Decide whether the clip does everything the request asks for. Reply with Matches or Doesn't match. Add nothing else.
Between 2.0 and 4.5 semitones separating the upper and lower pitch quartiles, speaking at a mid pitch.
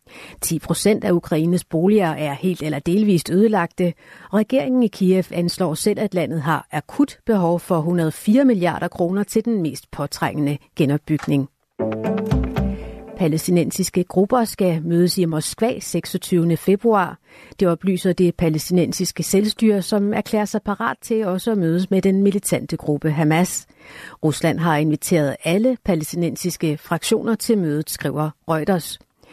Matches